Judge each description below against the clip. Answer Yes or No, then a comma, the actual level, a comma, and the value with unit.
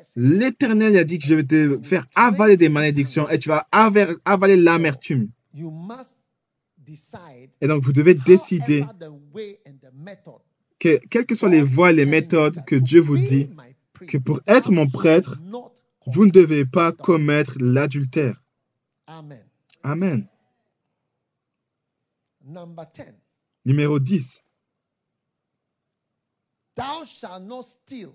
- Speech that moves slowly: Yes, slow, 100 wpm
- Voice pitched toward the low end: No, medium, 160 Hz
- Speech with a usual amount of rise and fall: Yes, average, 4.7 semitones